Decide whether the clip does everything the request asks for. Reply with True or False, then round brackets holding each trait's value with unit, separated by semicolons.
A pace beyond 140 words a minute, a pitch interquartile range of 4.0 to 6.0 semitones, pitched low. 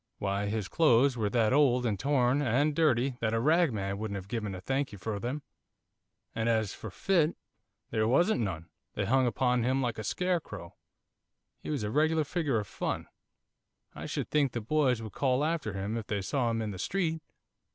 True (195 wpm; 5.2 semitones; 120 Hz)